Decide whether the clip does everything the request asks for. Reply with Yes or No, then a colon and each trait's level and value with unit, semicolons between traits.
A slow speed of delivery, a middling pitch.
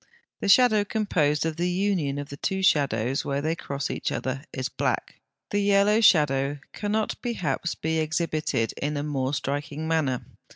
No: average, 170 wpm; medium, 155 Hz